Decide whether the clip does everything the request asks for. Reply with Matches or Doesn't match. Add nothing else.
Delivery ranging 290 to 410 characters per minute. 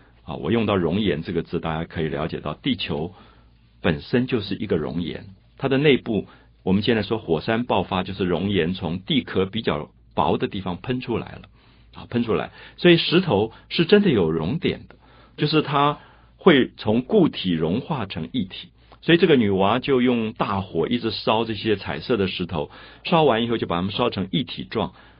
Doesn't match